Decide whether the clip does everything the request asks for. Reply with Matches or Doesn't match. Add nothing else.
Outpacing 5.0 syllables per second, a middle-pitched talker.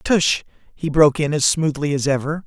Matches